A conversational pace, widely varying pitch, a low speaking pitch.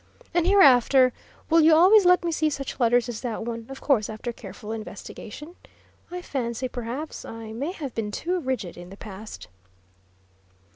No: average, 165 wpm; wide, 5.9 semitones; very high, 255 Hz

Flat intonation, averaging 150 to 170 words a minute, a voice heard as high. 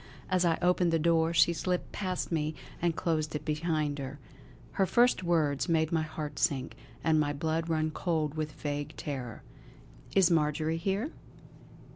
No: narrow, 2.1 semitones; average, 160 wpm; medium, 160 Hz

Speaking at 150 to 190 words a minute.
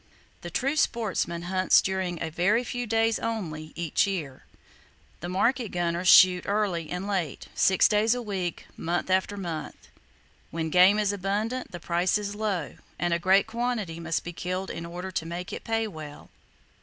Yes: average, 170 wpm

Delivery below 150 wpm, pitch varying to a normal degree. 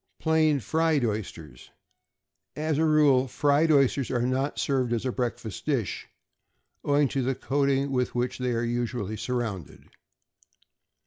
Yes: slow, 135 wpm; average, 3.1 semitones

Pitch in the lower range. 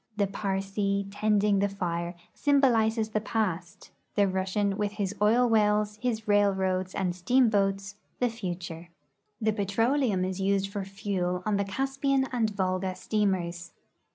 No: high, 200 Hz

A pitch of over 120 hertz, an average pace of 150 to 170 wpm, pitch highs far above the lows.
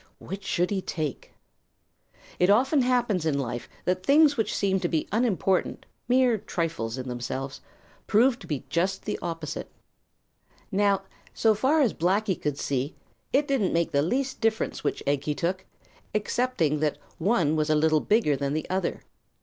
Yes: medium, 185 Hz; average, 165 wpm; wide, 6.6 semitones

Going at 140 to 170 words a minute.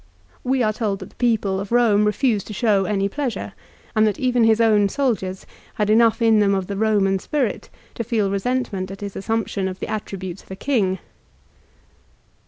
No: average, 190 wpm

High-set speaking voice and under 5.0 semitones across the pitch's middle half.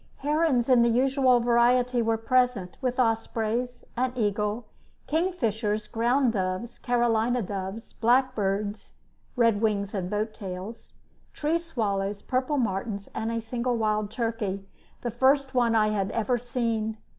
Yes: high, 230 Hz; average, 2.9 semitones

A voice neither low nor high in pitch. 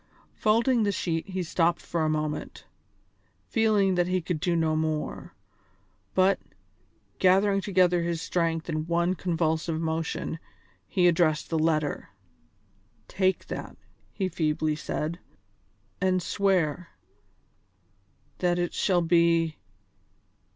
Yes: medium, 170 Hz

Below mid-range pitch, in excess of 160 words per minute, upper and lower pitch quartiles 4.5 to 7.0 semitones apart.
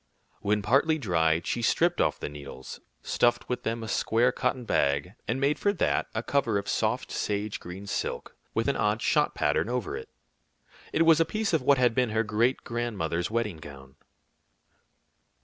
Yes: low, 115 Hz; average, 180 wpm; wide, 5.5 semitones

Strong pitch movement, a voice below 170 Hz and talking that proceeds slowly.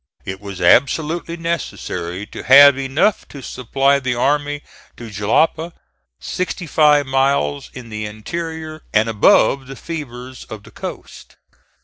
Yes: wide, 6.1 semitones; low, 135 Hz; slow, 130 wpm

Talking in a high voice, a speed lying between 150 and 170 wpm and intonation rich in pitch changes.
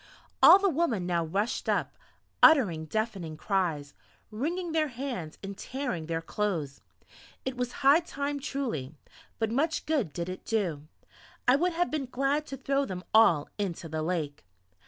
Yes: high, 220 Hz; average, 155 wpm; wide, 8.9 semitones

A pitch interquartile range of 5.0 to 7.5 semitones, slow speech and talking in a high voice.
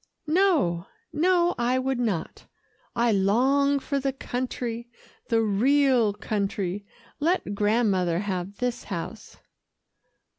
Yes: wide, 5.4 semitones; slow, 105 wpm; high, 235 Hz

